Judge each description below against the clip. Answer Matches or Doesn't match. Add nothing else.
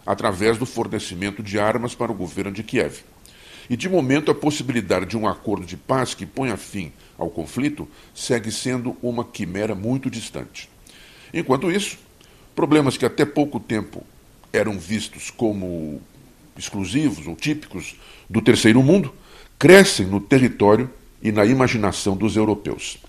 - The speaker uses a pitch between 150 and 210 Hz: Doesn't match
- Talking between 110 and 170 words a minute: Matches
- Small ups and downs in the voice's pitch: Doesn't match